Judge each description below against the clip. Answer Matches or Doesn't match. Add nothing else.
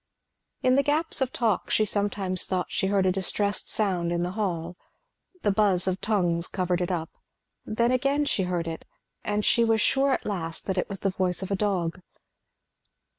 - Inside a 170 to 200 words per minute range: Matches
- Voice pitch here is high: Matches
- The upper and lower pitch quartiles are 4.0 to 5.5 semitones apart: Doesn't match